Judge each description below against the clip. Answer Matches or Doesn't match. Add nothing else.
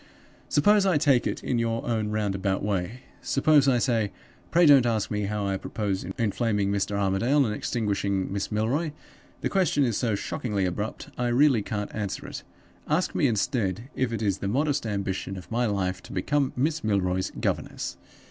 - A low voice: Matches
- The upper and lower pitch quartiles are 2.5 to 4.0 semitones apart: Doesn't match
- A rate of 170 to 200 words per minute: Matches